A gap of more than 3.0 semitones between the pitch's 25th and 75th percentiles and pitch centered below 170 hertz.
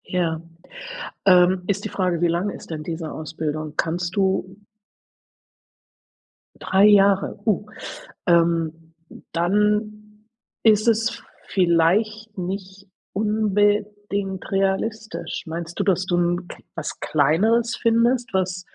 No: average, 3.5 semitones; high, 190 Hz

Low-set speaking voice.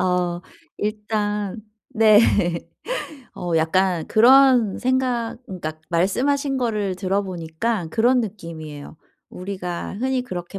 No: high, 205 Hz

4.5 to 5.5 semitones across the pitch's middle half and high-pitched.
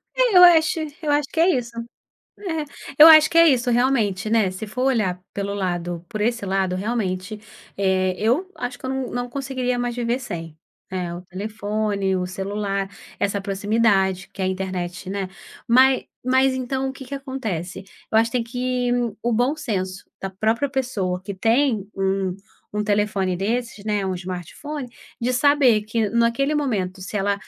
Yes: average, 5.1 semitones; high, 220 Hz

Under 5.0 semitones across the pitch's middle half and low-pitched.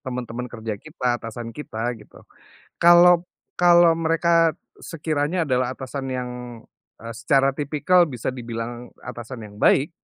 No: wide, 5.4 semitones; low, 130 Hz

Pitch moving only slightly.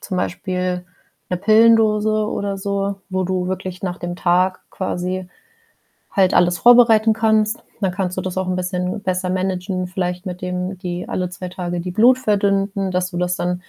Yes: narrow, 1.8 semitones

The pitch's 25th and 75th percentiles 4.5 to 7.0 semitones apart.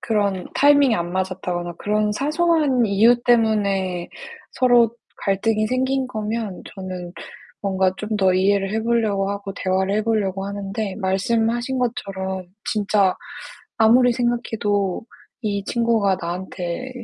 No: average, 3.6 semitones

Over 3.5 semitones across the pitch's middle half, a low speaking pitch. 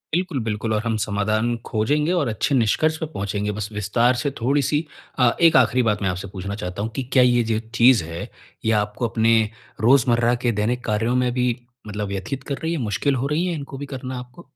Yes: average, 4.2 semitones; low, 120 Hz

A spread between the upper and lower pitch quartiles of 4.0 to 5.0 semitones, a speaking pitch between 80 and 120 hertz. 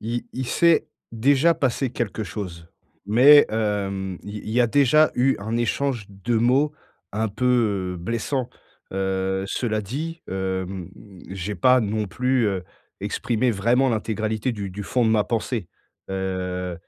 Yes: average, 4.5 semitones; low, 110 Hz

